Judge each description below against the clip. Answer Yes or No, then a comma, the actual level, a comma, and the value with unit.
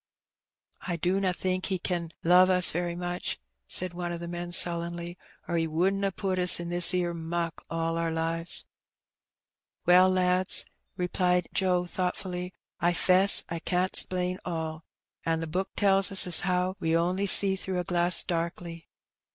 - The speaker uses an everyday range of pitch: No, narrow, 1.4 semitones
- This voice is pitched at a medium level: Yes, medium, 180 Hz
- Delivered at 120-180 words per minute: Yes, average, 165 wpm